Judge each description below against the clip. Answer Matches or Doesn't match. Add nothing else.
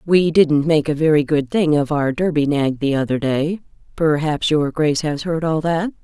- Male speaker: Doesn't match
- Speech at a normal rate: Doesn't match